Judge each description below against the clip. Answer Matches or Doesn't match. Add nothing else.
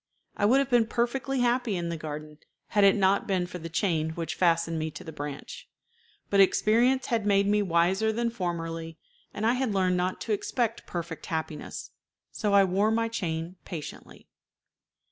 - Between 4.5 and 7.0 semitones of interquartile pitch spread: Matches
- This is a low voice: Doesn't match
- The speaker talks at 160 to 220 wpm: Matches